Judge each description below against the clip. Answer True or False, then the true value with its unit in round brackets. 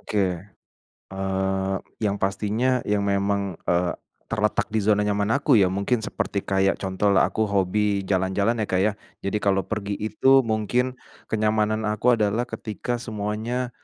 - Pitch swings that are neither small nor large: False (2.0 semitones)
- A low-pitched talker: True (105 Hz)